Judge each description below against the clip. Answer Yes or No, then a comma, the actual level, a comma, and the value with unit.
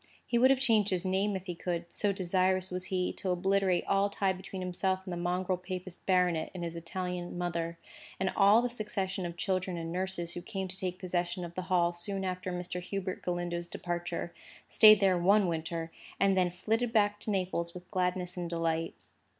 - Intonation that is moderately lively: No, narrow, 1.7 semitones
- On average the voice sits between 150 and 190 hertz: Yes, medium, 185 Hz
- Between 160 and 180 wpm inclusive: No, average, 200 wpm